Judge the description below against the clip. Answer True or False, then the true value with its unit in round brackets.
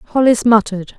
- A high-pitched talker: True (220 Hz)